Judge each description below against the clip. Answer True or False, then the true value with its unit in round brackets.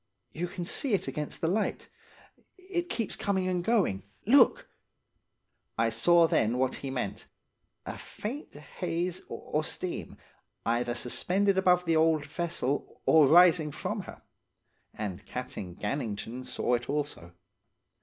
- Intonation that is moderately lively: False (6.5 semitones)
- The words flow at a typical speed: False (130 wpm)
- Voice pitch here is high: False (160 Hz)